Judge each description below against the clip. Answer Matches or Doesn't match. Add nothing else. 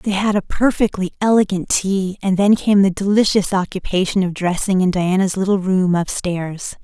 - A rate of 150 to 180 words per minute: Matches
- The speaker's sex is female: Matches